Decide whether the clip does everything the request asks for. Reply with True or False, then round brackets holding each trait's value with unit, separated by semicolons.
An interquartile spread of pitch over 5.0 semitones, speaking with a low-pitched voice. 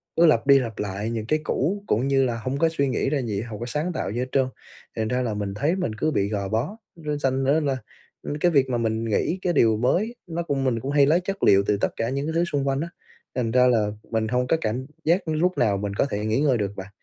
True (5.4 semitones; 130 Hz)